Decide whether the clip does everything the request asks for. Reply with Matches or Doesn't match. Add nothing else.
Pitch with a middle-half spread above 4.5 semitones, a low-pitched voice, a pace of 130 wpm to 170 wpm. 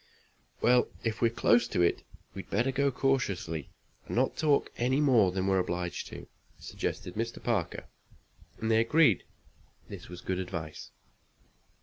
Matches